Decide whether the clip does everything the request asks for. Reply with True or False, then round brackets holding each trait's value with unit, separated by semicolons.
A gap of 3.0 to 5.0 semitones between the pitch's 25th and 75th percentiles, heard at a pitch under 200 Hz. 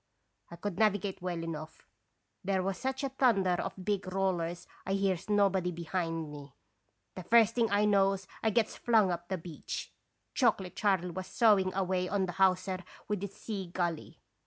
False (2.4 semitones; 190 Hz)